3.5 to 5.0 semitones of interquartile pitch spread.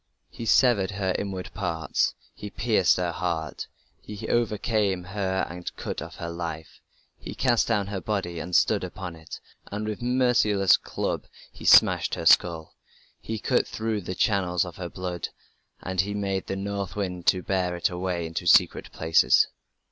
No: average, 2.9 semitones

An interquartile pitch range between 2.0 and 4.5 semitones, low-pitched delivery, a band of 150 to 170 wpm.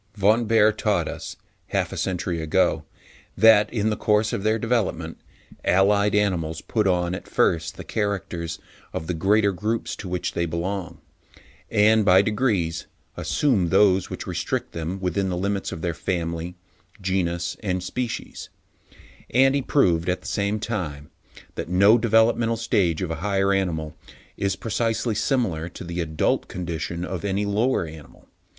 Yes: average, 3.8 semitones; very low, 95 Hz; average, 155 wpm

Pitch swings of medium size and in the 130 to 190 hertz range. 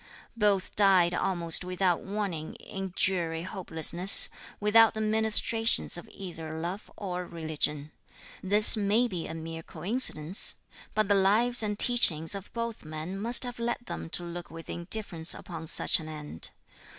Yes: average, 4.5 semitones; medium, 185 Hz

